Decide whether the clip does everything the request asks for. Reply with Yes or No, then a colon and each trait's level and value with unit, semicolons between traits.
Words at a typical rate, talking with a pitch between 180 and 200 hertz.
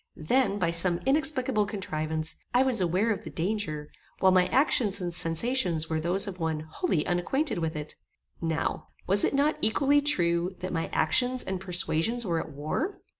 Yes: average, 175 wpm; medium, 185 Hz